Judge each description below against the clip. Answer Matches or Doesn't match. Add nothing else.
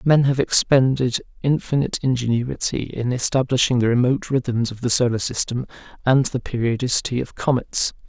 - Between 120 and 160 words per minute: Matches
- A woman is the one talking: Doesn't match